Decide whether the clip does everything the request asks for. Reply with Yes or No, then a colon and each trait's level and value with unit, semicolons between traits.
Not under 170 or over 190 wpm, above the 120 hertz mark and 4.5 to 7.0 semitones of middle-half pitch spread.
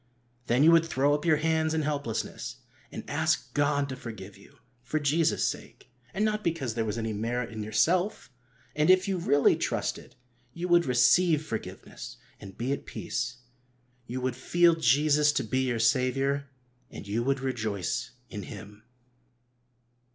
No: average, 160 wpm; low, 135 Hz; average, 5.2 semitones